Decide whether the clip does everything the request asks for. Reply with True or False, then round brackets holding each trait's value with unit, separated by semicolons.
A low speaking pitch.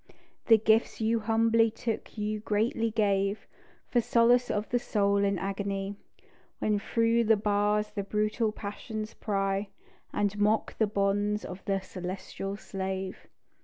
False (210 Hz)